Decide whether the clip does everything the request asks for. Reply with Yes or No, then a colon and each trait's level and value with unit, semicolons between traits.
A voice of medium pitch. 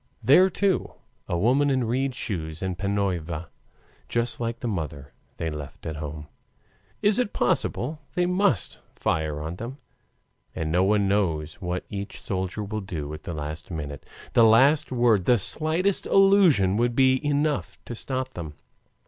No: low, 105 Hz